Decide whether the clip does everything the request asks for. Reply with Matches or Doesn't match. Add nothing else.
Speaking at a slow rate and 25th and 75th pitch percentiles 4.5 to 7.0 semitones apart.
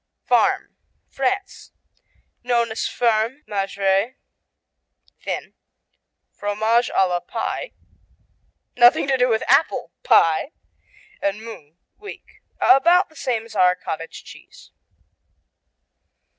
Matches